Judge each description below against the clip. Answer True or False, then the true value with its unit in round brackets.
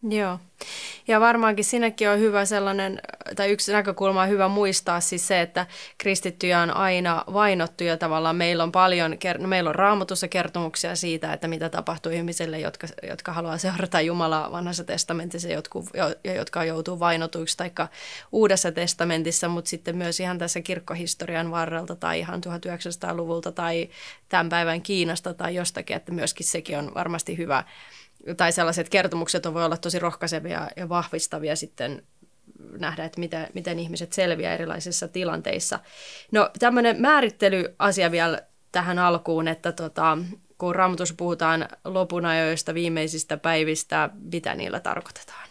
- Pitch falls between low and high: True (175 Hz)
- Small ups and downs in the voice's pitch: True (2.0 semitones)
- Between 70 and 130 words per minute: False (140 wpm)